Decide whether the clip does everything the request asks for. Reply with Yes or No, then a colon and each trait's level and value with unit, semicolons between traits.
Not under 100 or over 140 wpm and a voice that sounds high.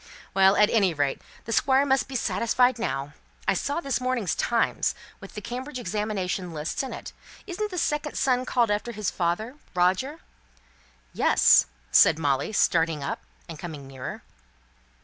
No: average, 155 wpm; high, 215 Hz